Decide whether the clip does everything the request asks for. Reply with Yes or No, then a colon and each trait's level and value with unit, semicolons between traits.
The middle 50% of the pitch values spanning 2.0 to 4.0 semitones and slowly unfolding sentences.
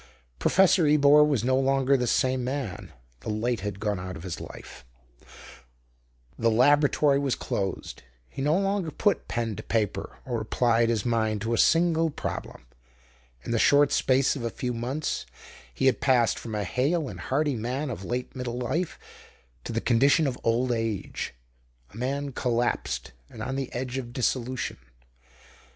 No: average, 3.6 semitones; average, 165 wpm